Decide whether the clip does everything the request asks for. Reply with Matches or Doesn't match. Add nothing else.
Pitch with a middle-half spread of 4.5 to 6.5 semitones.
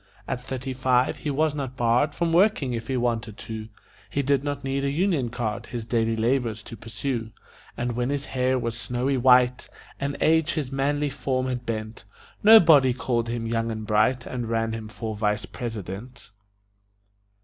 Doesn't match